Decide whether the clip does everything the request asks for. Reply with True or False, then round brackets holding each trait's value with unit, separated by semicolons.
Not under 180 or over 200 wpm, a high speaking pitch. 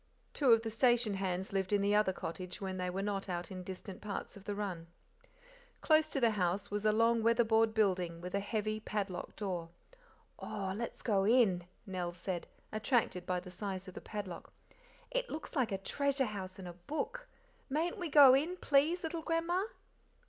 True (190 wpm; 205 Hz)